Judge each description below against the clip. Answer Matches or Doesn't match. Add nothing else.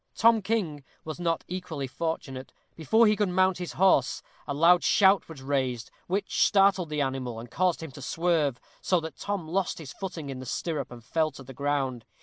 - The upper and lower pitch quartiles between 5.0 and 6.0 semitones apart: Matches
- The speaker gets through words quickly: Doesn't match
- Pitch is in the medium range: Matches